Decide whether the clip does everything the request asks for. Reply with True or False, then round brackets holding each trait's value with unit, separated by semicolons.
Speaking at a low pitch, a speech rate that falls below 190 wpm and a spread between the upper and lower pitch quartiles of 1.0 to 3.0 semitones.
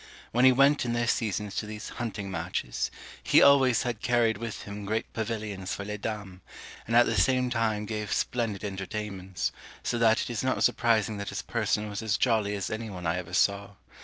False (110 Hz; 200 wpm; 2.6 semitones)